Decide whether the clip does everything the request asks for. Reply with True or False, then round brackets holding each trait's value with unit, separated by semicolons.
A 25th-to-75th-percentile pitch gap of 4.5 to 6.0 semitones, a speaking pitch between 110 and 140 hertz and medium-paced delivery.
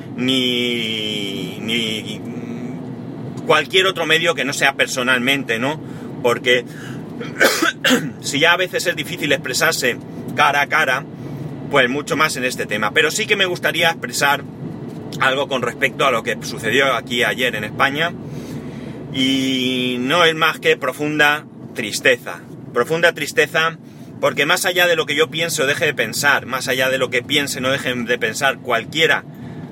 False (4.0 semitones; 135 Hz; 150 wpm)